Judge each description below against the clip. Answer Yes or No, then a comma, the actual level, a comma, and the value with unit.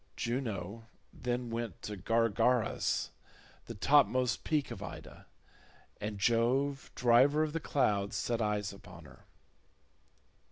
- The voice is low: Yes, low, 115 Hz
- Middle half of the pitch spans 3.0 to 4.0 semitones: Yes, average, 3.6 semitones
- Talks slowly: Yes, slow, 115 wpm